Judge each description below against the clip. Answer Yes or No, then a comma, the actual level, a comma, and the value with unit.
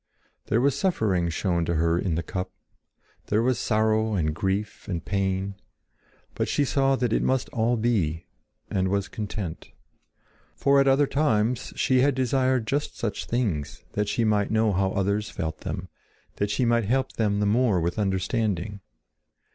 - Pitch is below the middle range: Yes, low, 105 Hz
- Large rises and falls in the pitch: No, average, 4.3 semitones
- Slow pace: No, average, 165 wpm